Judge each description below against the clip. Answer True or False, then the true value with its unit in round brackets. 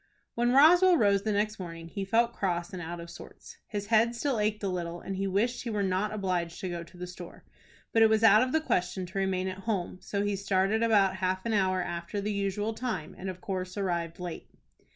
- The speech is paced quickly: True (235 wpm)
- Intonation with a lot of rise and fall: False (3.0 semitones)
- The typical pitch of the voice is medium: False (195 Hz)